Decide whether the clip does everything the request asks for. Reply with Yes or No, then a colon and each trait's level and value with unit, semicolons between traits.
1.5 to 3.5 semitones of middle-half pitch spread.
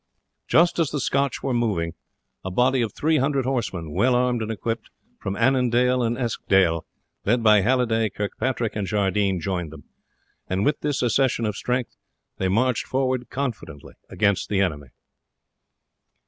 No: average, 4.7 semitones